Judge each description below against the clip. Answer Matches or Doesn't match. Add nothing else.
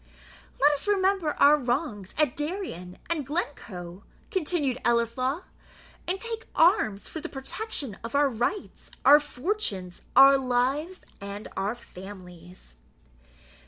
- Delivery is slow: Matches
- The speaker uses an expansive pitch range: Matches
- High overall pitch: Matches